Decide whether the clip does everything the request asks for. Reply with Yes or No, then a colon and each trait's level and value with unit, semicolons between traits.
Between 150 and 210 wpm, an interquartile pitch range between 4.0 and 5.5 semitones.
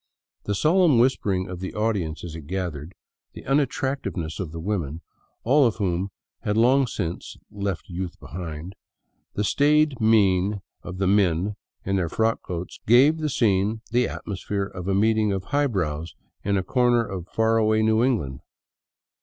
Yes: average, 165 wpm; average, 4.4 semitones